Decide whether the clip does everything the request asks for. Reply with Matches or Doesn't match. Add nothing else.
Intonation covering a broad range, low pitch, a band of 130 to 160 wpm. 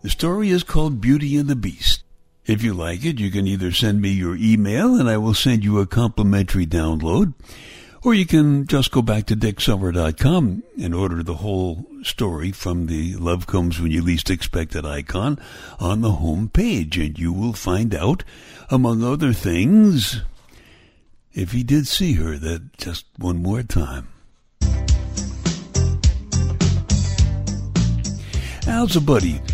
Matches